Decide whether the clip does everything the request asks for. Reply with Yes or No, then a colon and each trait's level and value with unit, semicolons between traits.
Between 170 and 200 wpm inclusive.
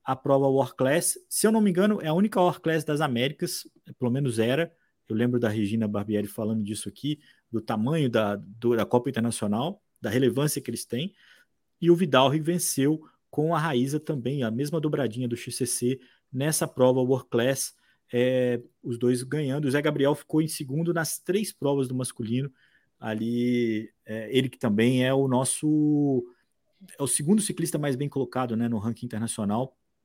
Yes: average, 180 wpm